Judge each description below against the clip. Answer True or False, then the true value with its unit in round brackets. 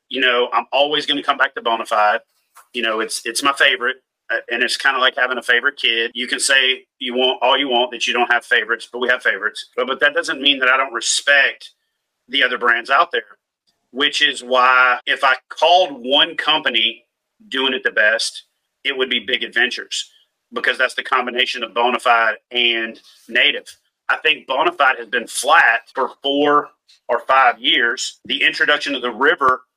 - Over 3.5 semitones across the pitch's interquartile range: False (2.8 semitones)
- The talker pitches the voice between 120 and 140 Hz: True (130 Hz)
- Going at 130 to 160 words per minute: False (200 wpm)